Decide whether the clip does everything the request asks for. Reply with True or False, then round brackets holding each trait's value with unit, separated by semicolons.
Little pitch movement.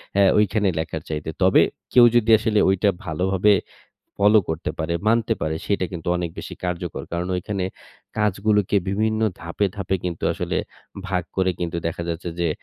False (3.4 semitones)